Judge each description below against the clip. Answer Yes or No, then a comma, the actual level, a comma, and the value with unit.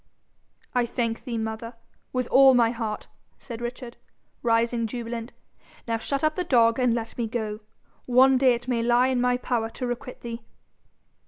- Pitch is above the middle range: Yes, high, 240 Hz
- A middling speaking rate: Yes, average, 170 wpm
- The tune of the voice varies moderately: No, narrow, 1.6 semitones